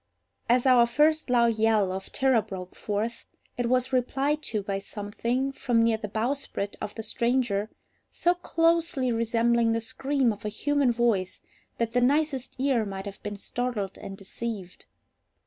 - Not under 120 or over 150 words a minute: No, average, 160 wpm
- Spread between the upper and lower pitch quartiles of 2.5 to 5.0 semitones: Yes, average, 3.8 semitones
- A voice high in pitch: Yes, high, 235 Hz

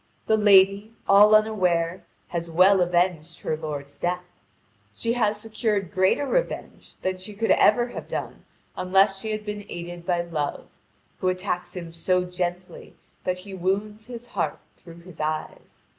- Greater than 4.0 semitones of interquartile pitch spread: No, average, 3.3 semitones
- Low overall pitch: No, medium, 185 Hz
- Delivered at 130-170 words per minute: Yes, average, 155 wpm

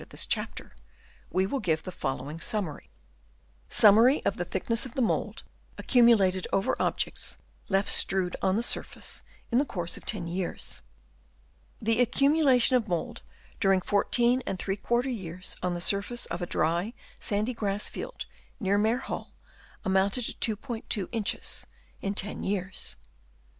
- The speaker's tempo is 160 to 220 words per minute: No, average, 145 wpm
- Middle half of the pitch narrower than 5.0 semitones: Yes, average, 4.3 semitones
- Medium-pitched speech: No, high, 205 Hz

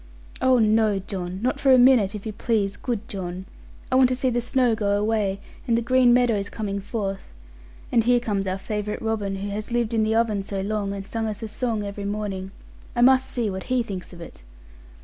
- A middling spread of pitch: Yes, average, 3.2 semitones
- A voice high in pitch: Yes, high, 215 Hz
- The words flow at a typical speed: No, fast, 220 wpm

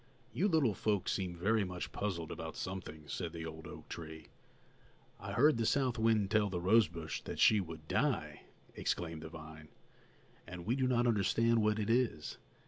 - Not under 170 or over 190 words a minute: Yes, average, 180 wpm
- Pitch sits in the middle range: No, very low, 95 Hz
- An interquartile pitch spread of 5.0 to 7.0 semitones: Yes, wide, 5.6 semitones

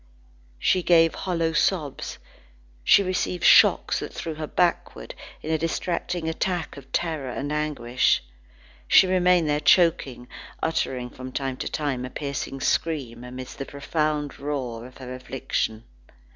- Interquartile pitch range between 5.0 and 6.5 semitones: No, average, 4.4 semitones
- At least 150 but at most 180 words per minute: No, average, 140 wpm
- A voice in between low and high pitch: Yes, medium, 150 Hz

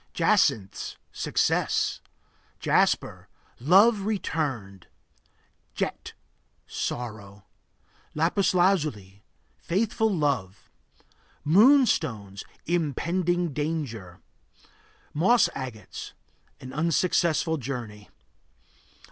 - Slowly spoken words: Yes, slow, 60 wpm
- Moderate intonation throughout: No, wide, 8.4 semitones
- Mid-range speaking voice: Yes, medium, 150 Hz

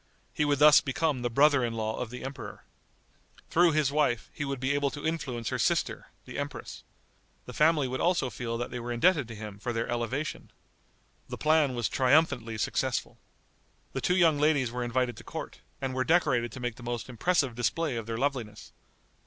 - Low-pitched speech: Yes, low, 130 Hz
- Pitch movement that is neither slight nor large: Yes, average, 3.9 semitones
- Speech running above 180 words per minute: Yes, average, 200 wpm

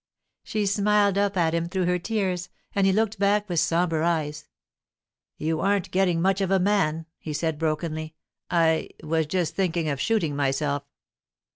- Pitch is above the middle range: No, medium, 175 Hz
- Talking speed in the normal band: Yes, average, 160 wpm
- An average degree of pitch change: Yes, average, 3.7 semitones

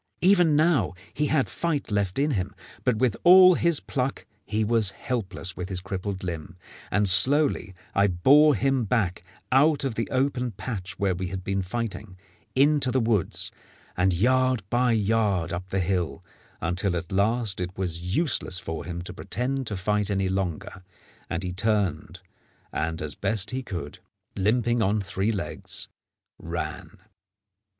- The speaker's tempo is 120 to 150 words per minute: No, average, 160 wpm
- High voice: No, low, 105 Hz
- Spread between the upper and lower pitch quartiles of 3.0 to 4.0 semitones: No, wide, 5.6 semitones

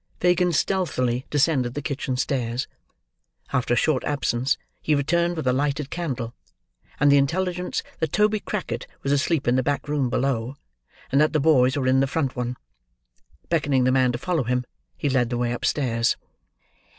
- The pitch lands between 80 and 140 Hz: Yes, low, 135 Hz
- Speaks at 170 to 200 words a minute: Yes, average, 175 wpm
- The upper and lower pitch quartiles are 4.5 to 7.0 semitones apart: No, average, 3.5 semitones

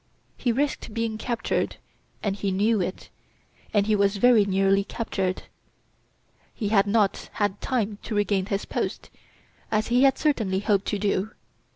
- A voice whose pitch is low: No, high, 205 Hz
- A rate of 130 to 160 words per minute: Yes, average, 155 wpm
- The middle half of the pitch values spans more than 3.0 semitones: No, narrow, 2.4 semitones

